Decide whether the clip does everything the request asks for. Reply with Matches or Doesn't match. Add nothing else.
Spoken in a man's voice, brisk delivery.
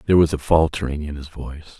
Matches